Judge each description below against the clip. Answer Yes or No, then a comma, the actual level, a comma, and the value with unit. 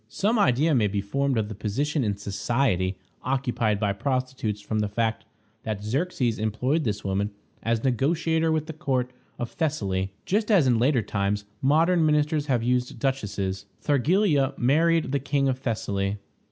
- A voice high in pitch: No, low, 125 Hz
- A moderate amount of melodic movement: No, wide, 5.9 semitones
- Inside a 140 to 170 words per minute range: Yes, average, 160 wpm